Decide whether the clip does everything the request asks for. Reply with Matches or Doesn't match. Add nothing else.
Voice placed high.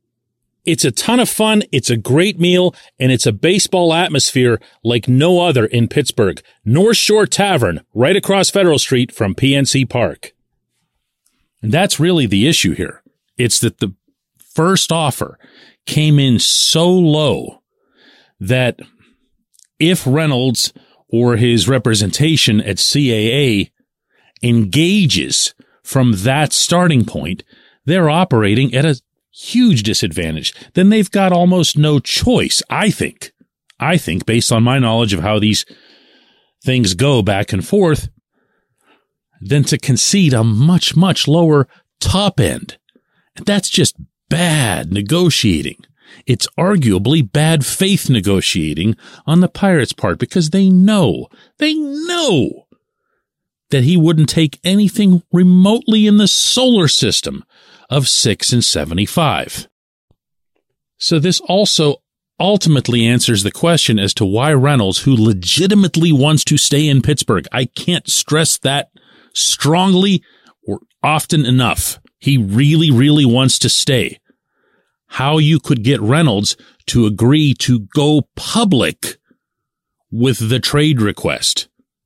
Doesn't match